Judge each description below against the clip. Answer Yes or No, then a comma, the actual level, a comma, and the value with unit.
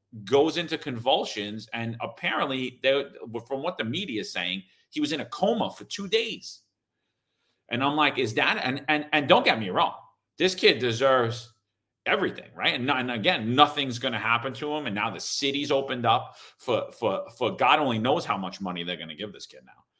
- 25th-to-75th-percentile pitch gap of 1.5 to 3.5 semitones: No, average, 4.8 semitones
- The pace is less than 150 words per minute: No, average, 200 wpm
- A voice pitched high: No, low, 130 Hz